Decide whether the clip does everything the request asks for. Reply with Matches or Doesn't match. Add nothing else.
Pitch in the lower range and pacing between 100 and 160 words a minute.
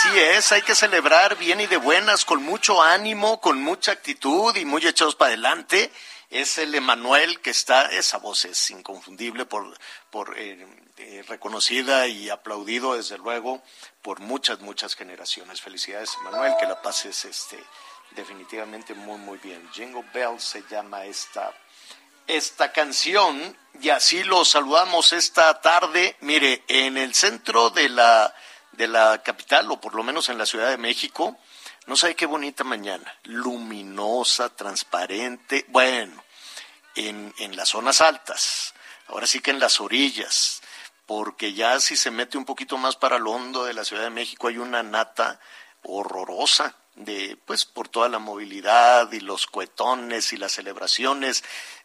Matches